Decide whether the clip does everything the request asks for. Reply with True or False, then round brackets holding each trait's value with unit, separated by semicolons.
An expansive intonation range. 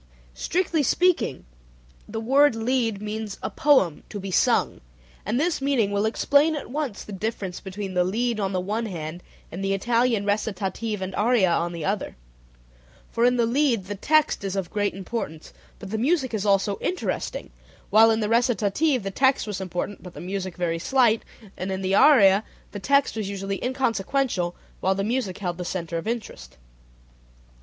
False (4.3 semitones)